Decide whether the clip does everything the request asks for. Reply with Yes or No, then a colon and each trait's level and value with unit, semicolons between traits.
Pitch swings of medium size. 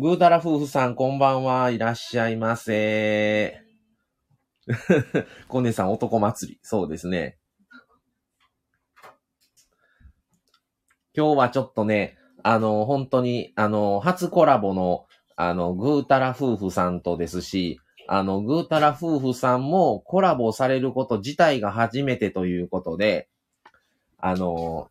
No: wide, 6.0 semitones